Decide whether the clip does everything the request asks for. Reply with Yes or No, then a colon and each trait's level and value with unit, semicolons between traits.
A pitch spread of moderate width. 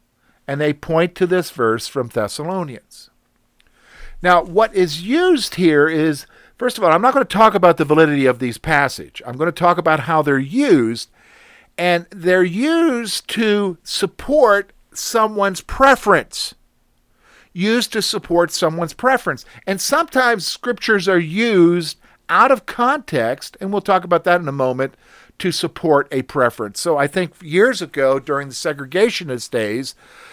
No: wide, 5.9 semitones